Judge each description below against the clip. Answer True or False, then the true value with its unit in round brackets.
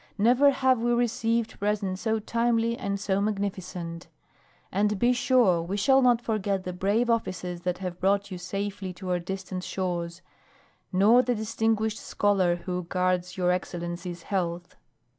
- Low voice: False (195 Hz)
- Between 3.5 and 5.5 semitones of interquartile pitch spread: True (3.8 semitones)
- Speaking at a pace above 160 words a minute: False (150 wpm)